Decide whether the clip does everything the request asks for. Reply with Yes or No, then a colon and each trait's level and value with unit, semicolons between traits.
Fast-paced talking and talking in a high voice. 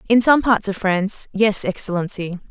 No: average, 145 wpm; high, 205 Hz